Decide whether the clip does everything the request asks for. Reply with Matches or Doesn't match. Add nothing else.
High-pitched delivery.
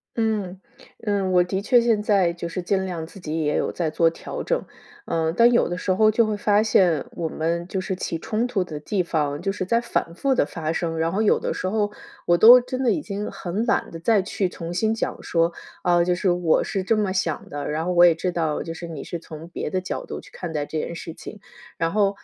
Doesn't match